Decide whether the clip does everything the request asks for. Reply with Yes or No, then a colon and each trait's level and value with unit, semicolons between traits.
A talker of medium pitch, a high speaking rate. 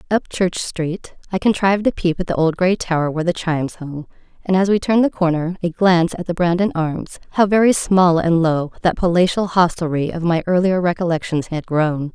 Yes: medium, 175 Hz; fast, 210 wpm